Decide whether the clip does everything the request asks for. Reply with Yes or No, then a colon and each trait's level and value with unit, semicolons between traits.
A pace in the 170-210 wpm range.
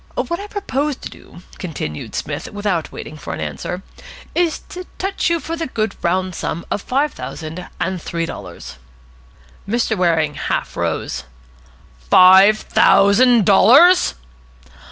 No: slow, 135 wpm